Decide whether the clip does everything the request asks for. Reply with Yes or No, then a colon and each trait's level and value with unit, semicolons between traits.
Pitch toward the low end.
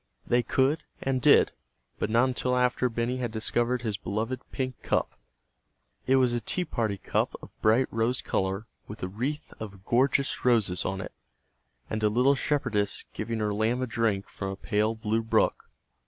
Yes: low, 115 Hz